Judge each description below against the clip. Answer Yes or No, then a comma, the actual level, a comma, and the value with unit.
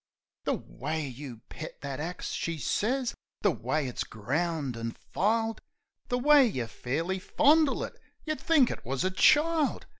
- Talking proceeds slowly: No, average, 155 wpm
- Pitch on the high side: No, medium, 170 Hz